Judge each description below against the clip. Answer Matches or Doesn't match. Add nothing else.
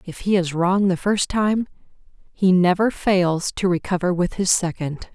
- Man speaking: Doesn't match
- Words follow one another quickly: Doesn't match